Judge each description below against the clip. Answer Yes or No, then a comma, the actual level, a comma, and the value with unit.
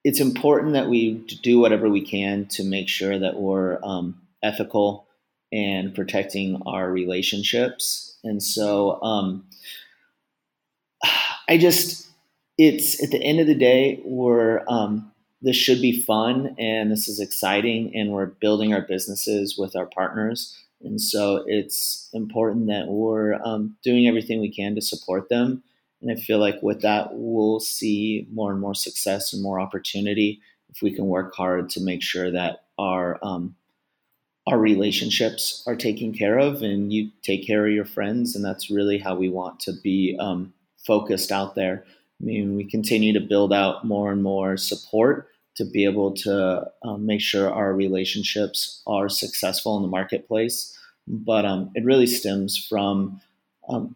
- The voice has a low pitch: Yes, low, 105 Hz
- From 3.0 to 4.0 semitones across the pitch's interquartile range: No, narrow, 2.5 semitones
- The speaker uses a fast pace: No, average, 160 wpm